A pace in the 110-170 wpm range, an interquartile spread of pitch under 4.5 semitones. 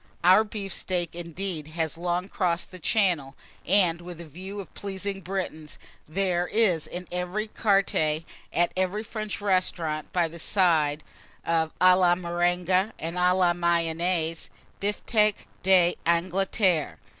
Yes: slow, 135 wpm; narrow, 2.4 semitones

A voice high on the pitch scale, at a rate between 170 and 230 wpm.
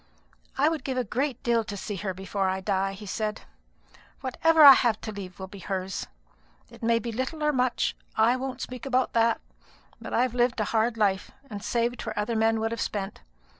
Yes: high, 225 Hz; fast, 205 wpm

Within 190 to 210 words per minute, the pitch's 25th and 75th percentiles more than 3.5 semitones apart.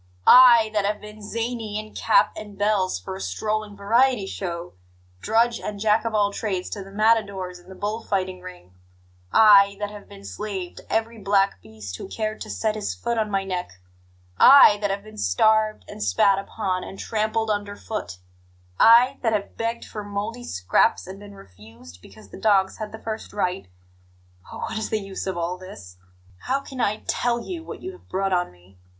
No: average, 195 wpm; average, 2.7 semitones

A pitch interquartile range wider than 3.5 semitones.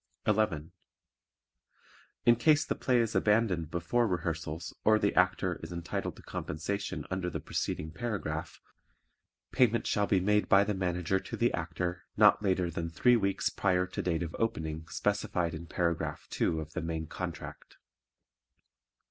Yes: average, 4.1 semitones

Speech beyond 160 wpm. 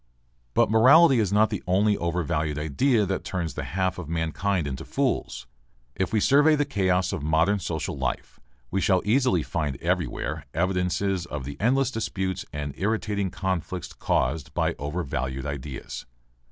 No: average, 155 wpm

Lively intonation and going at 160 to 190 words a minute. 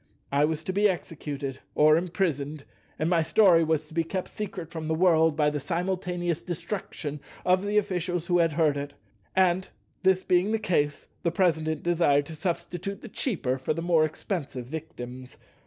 No: average, 3.3 semitones; average, 175 wpm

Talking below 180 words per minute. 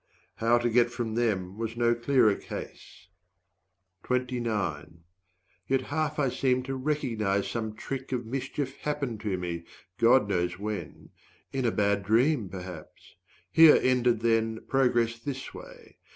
Yes: slow, 135 wpm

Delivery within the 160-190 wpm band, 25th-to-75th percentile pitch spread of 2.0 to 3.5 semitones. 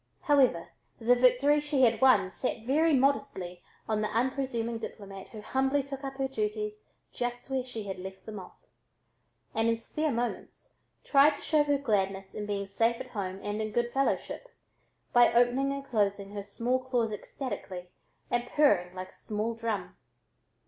No: average, 170 wpm; average, 4.4 semitones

